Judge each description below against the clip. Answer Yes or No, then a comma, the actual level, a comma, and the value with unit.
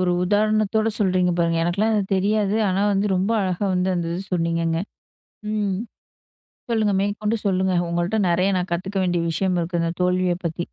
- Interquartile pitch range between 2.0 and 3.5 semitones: Yes, average, 2.8 semitones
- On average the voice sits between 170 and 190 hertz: Yes, medium, 185 Hz